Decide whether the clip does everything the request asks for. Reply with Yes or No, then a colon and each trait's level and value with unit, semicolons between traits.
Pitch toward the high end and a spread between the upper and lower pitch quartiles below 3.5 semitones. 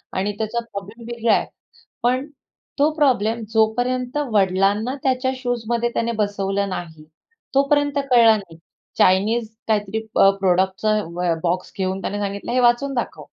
No: high, 220 Hz; average, 3.8 semitones